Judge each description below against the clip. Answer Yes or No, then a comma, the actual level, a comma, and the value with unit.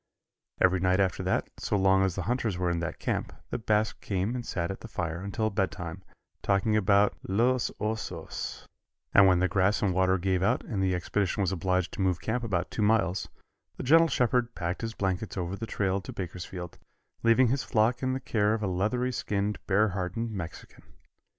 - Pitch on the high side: No, low, 100 Hz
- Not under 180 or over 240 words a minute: Yes, average, 195 wpm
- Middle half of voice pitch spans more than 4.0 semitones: No, average, 3.3 semitones